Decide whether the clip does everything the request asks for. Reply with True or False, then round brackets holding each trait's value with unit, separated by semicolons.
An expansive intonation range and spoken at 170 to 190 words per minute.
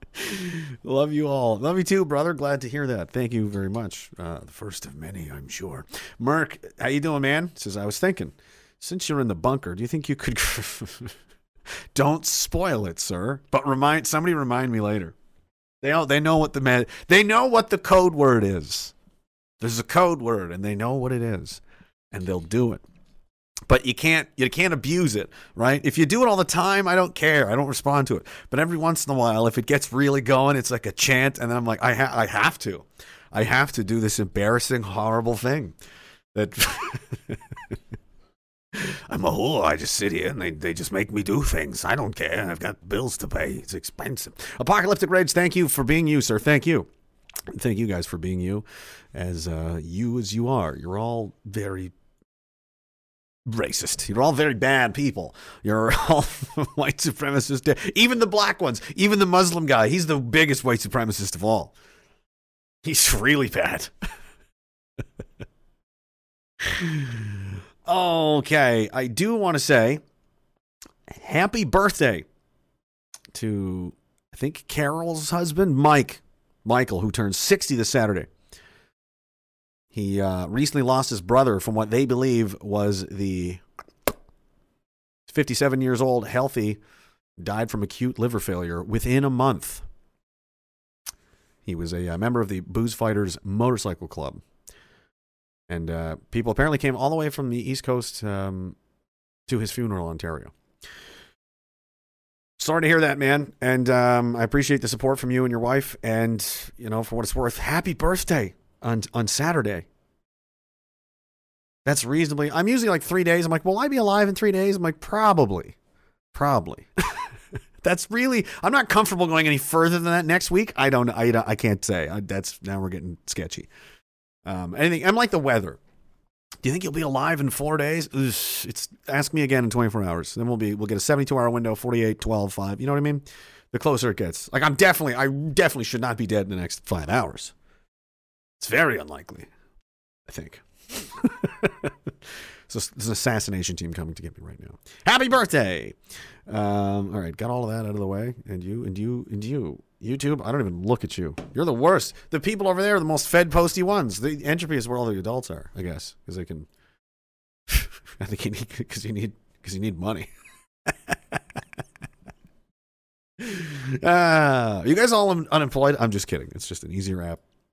True (6.8 semitones; 180 wpm)